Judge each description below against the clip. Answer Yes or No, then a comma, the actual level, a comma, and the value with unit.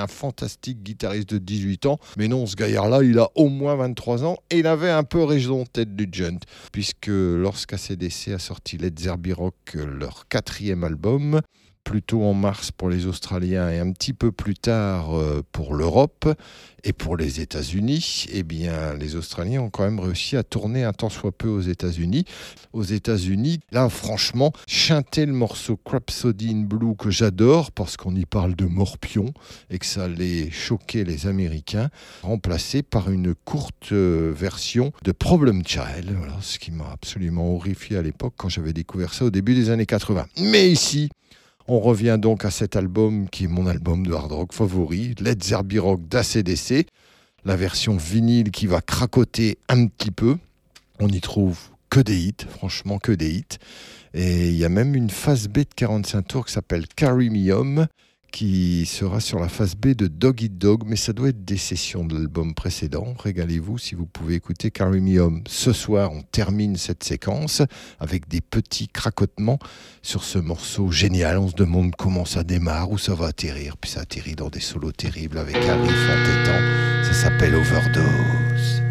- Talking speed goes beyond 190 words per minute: No, average, 180 wpm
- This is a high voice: No, low, 100 Hz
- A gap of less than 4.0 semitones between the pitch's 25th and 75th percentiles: No, average, 4.9 semitones